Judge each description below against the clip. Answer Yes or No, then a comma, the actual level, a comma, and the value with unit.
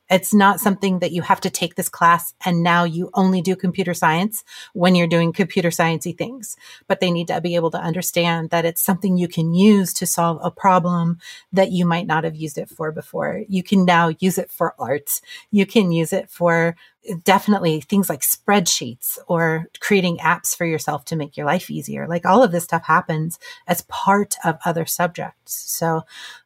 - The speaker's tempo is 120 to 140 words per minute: No, average, 200 wpm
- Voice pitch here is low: No, medium, 175 Hz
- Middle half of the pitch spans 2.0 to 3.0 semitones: Yes, narrow, 2.5 semitones